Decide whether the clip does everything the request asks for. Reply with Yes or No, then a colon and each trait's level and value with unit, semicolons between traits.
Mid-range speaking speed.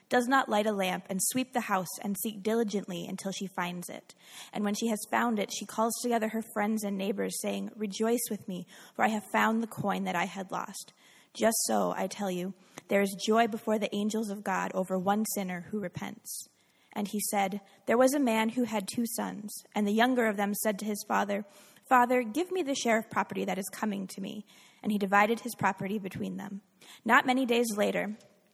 No: fast, 220 wpm